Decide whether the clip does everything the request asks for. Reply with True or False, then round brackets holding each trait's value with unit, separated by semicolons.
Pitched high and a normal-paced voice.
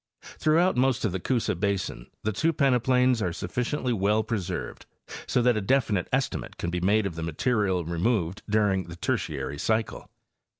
False (105 Hz; 170 wpm)